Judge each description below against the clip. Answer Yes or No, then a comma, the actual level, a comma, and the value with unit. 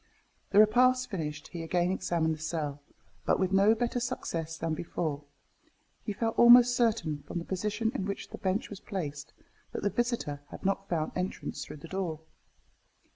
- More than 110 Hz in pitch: Yes, high, 190 Hz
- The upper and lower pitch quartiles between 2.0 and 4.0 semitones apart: No, wide, 5.5 semitones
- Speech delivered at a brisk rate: No, average, 180 wpm